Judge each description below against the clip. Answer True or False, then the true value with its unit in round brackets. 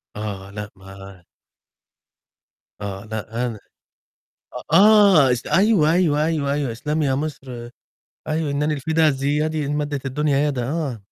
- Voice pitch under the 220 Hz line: True (140 Hz)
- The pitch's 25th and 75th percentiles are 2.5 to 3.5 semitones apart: False (4.8 semitones)